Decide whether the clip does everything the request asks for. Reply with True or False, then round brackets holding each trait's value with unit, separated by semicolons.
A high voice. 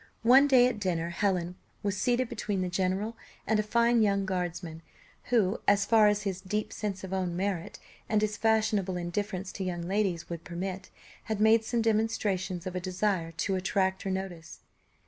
True (195 Hz)